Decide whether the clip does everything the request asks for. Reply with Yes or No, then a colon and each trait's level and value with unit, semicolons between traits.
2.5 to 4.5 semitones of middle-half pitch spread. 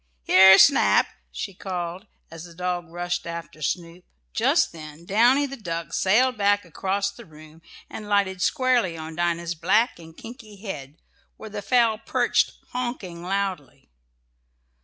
Yes: average, 3.9 semitones